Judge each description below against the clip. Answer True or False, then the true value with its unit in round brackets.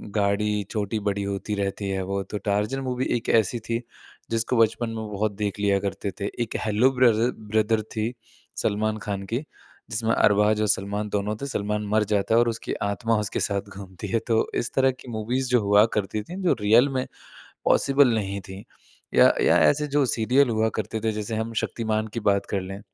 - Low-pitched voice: True (110 Hz)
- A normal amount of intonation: False (2.3 semitones)